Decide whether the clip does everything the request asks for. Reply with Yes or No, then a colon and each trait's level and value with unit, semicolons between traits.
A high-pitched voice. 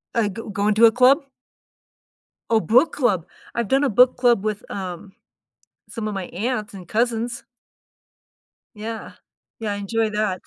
Yes: high, 220 Hz